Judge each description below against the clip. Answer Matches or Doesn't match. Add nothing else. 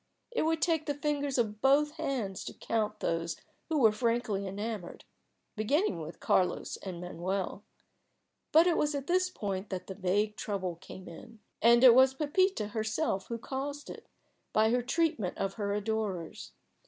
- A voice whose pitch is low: Doesn't match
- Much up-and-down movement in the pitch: Matches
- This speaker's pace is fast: Doesn't match